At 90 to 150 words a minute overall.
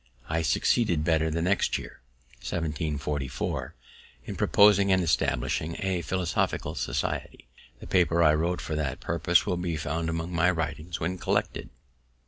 Yes: average, 140 wpm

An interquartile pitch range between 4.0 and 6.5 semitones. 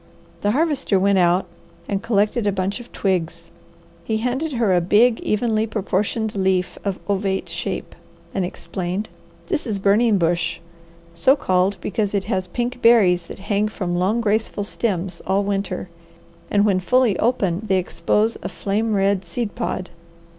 No: average, 3.1 semitones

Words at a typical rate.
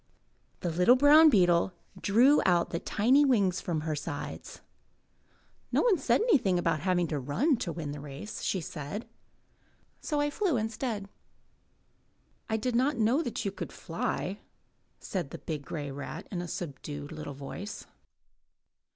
Yes: average, 150 wpm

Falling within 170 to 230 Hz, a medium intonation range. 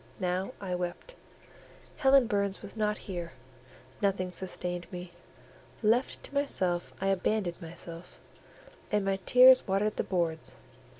Yes: high, 190 Hz; average, 3.1 semitones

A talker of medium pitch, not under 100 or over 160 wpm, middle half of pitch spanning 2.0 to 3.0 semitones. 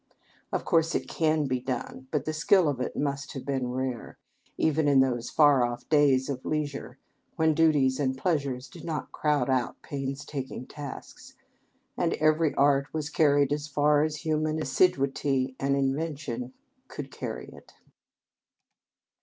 Yes: medium, 145 Hz; average, 150 wpm; average, 2.7 semitones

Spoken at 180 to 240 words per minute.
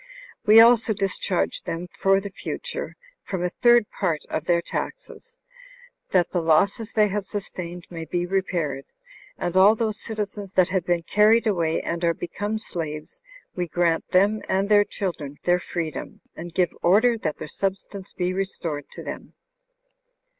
No: average, 160 wpm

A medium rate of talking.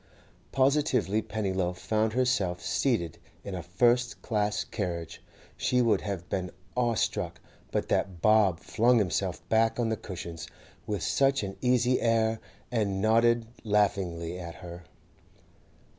No: slow, 130 wpm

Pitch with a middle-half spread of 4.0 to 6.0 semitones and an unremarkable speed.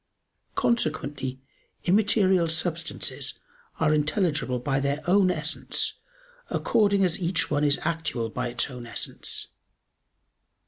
No: average, 5.0 semitones; slow, 105 wpm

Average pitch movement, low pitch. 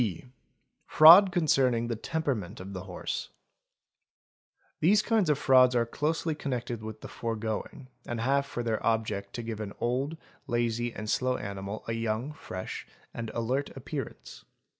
Yes: average, 4.2 semitones; low, 120 Hz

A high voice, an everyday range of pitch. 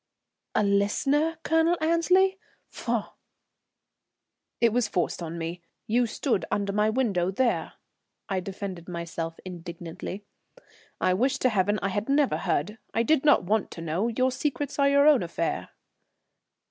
No: high, 210 Hz; wide, 7.3 semitones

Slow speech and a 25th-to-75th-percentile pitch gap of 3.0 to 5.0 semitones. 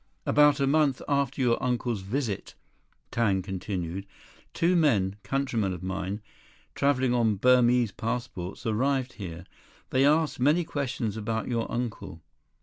No: slow, 130 wpm; wide, 5.4 semitones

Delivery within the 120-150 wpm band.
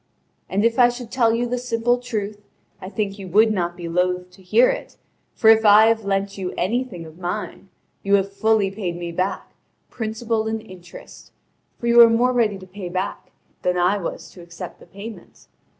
No: average, 200 wpm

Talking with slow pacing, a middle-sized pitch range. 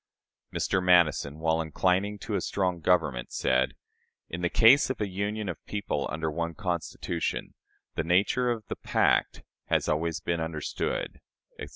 No: average, 160 wpm; average, 3.9 semitones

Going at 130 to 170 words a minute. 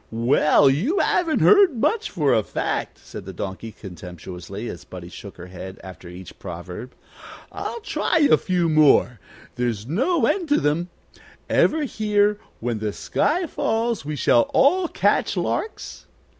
Yes: average, 150 wpm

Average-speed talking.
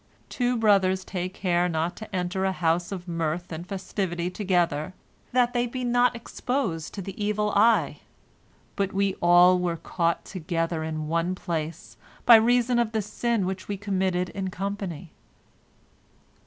Yes: average, 155 wpm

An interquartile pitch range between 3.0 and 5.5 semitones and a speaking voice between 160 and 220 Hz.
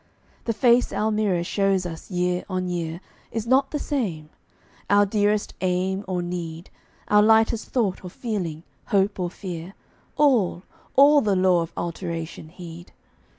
Yes: average, 3.6 semitones; high, 190 Hz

